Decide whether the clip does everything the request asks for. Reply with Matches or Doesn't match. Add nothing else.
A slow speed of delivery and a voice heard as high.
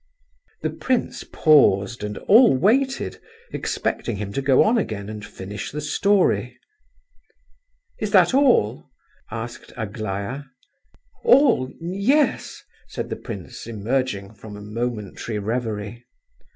Doesn't match